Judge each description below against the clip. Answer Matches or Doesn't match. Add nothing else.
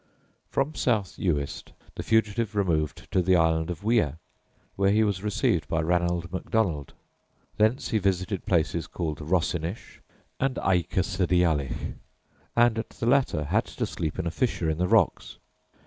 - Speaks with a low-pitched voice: Matches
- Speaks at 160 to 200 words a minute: Doesn't match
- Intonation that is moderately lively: Matches